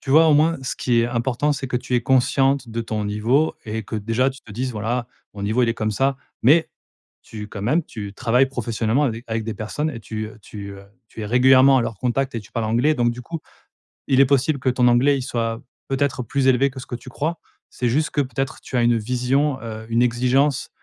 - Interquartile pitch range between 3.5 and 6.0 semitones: No, average, 3.0 semitones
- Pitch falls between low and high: No, low, 125 Hz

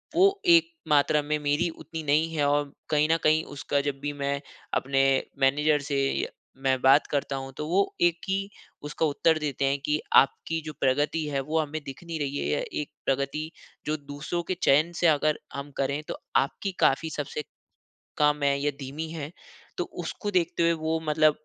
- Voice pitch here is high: No, medium, 150 Hz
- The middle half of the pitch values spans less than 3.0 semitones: Yes, narrow, 2.4 semitones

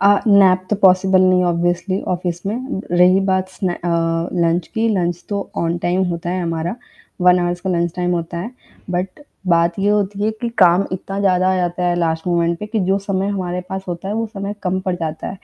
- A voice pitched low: No, medium, 185 Hz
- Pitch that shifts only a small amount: Yes, narrow, 2.0 semitones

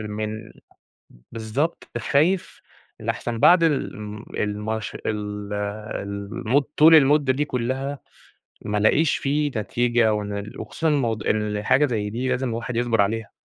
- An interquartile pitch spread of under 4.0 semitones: No, average, 4.7 semitones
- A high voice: No, low, 115 Hz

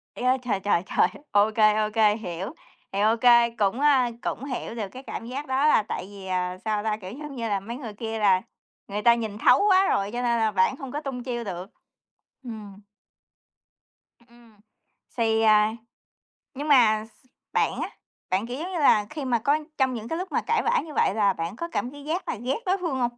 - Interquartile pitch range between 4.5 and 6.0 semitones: No, average, 4.1 semitones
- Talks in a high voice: Yes, high, 230 Hz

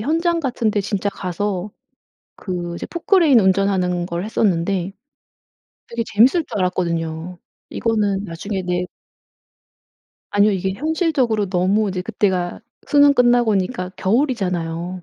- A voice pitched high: Yes, high, 200 Hz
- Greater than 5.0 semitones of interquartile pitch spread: No, average, 4.4 semitones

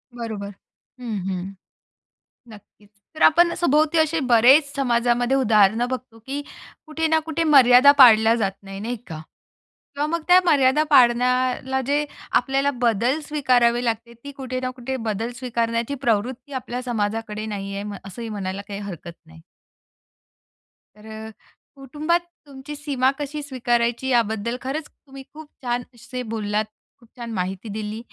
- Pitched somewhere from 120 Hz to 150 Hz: No, high, 245 Hz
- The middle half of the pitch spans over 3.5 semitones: Yes, average, 4.0 semitones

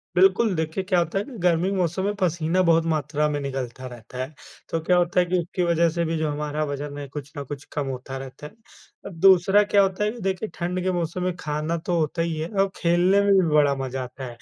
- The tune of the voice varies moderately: Yes, average, 3.9 semitones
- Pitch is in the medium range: Yes, medium, 165 Hz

